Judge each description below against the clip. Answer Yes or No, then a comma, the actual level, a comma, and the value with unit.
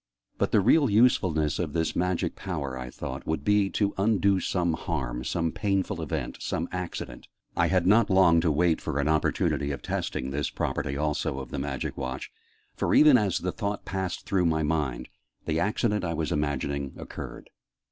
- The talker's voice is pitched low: Yes, very low, 85 Hz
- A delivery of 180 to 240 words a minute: Yes, average, 185 wpm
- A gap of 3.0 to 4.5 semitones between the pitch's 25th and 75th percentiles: No, average, 5.0 semitones